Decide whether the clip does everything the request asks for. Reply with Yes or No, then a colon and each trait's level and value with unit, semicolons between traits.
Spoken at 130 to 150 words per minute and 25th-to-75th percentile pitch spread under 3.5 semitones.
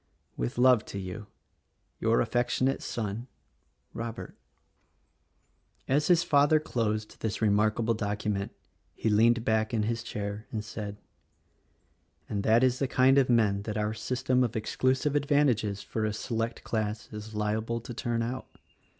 Yes: average, 140 wpm; average, 2.8 semitones